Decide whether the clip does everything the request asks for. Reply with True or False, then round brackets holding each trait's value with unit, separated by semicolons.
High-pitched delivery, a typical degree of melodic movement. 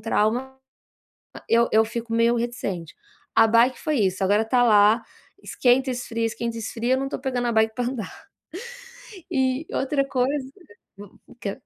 False (235 Hz; 2.3 semitones)